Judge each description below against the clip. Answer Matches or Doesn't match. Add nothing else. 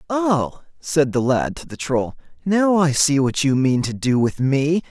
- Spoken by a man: Matches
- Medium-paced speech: Doesn't match